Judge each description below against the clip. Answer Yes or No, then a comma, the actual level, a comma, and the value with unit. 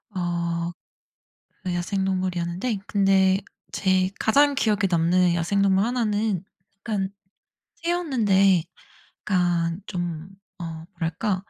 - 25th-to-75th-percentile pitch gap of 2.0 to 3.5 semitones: Yes, average, 2.9 semitones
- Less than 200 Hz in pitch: Yes, high, 190 Hz